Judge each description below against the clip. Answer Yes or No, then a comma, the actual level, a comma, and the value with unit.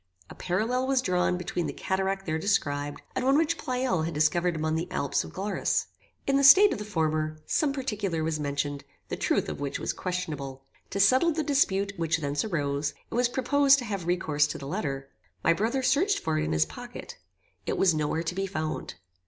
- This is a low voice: No, medium, 180 Hz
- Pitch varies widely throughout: Yes, wide, 7.7 semitones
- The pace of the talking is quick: Yes, fast, 210 wpm